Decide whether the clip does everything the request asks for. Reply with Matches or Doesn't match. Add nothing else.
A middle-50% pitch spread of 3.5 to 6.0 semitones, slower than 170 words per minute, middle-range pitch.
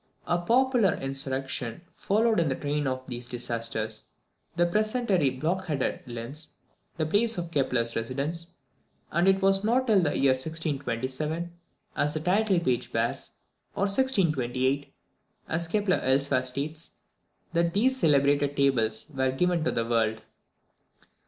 Matches